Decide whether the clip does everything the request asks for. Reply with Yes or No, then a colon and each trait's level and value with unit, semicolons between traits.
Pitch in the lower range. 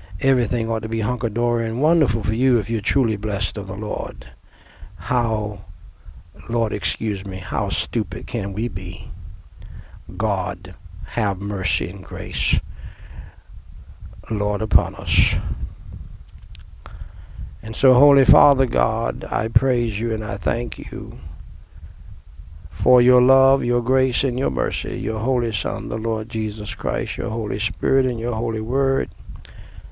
Yes: low, 100 Hz